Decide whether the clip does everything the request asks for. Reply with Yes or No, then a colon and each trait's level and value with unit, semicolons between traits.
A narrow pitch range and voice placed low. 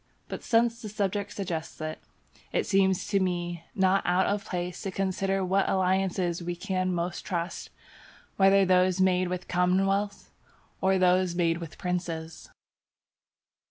No: narrow, 1.7 semitones; medium, 185 Hz